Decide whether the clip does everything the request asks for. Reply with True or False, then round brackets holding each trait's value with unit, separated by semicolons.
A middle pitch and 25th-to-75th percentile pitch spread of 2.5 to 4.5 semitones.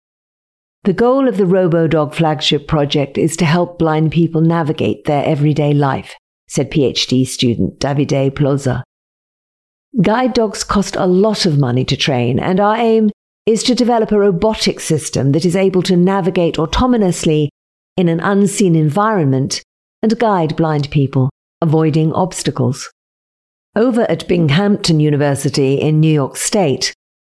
False (160 Hz; 5.2 semitones)